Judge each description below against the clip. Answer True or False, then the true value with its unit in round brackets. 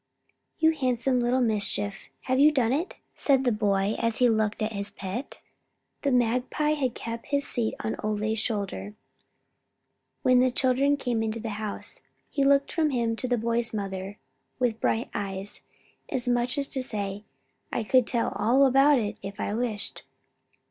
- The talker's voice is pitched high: True (235 Hz)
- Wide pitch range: False (3.5 semitones)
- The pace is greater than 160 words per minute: True (170 wpm)